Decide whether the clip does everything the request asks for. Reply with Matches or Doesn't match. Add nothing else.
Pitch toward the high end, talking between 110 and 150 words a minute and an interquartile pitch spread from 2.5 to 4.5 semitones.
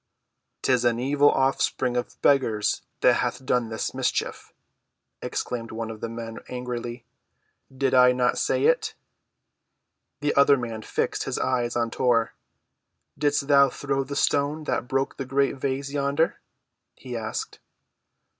Doesn't match